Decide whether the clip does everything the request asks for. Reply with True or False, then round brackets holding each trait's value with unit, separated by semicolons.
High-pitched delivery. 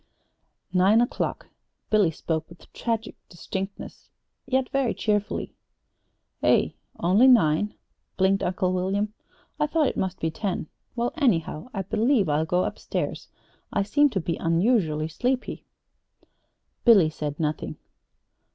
True (195 Hz)